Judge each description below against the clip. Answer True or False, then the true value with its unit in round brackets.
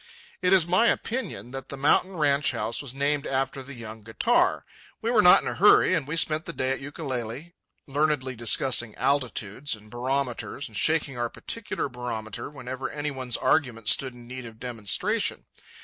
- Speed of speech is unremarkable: True (180 wpm)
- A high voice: False (135 Hz)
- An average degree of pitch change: True (3.8 semitones)